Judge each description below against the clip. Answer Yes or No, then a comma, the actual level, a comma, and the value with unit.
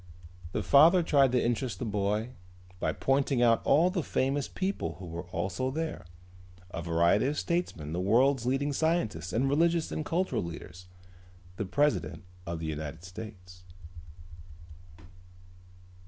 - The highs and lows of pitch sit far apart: Yes, wide, 8.1 semitones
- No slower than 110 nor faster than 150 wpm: Yes, average, 140 wpm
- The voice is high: No, low, 120 Hz